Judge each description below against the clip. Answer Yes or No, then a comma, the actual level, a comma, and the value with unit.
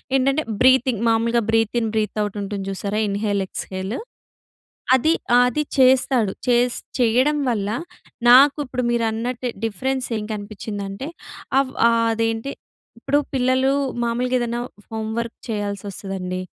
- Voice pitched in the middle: No, high, 230 Hz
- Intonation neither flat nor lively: Yes, average, 3.4 semitones